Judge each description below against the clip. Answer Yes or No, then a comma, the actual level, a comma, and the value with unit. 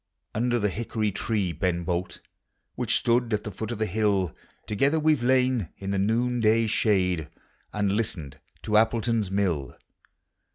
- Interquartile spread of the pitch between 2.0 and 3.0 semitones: No, average, 3.5 semitones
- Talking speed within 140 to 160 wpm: Yes, average, 155 wpm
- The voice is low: Yes, low, 105 Hz